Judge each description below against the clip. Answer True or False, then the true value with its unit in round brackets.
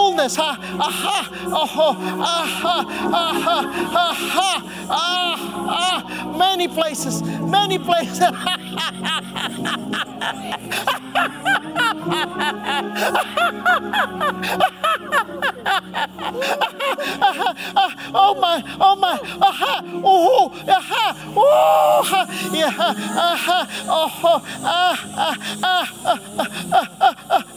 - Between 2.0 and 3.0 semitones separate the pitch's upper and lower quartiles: True (2.6 semitones)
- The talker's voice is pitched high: True (360 Hz)